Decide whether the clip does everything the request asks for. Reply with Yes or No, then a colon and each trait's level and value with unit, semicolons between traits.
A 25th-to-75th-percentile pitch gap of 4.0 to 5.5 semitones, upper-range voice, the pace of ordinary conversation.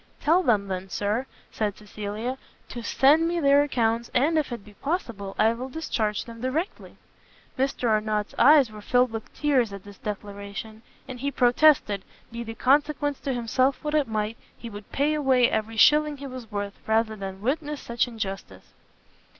Yes: average, 4.7 semitones; high, 235 Hz; average, 175 wpm